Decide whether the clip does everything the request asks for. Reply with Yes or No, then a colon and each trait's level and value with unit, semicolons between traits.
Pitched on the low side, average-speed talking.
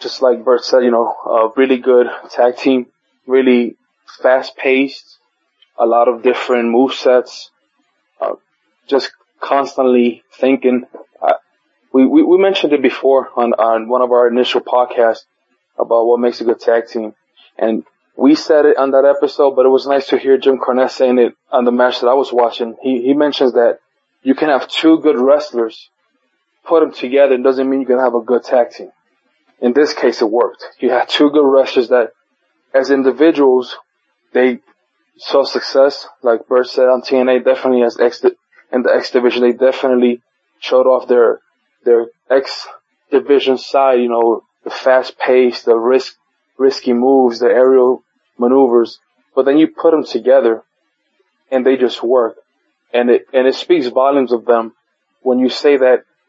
Yes: low, 130 Hz; average, 175 wpm